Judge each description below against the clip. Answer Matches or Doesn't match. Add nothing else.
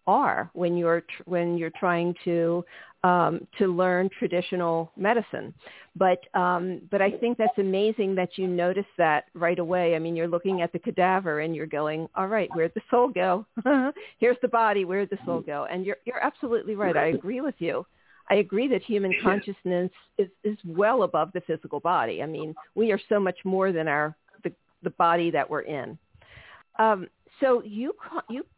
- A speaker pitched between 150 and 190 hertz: Matches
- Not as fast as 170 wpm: Doesn't match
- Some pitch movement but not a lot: Matches